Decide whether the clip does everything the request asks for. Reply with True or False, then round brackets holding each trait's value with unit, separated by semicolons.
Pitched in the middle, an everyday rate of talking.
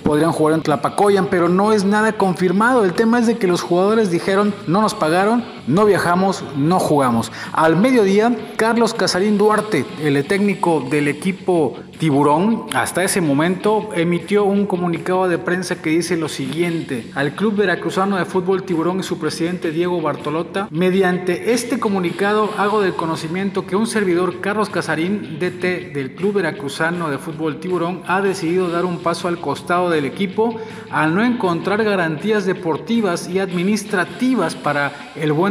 True (180 Hz; 160 wpm)